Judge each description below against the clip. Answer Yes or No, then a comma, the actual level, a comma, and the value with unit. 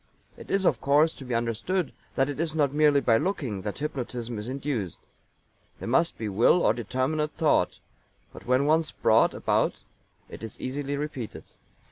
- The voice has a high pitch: No, low, 135 Hz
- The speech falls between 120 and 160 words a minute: No, average, 170 wpm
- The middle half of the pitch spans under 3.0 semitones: No, average, 4.6 semitones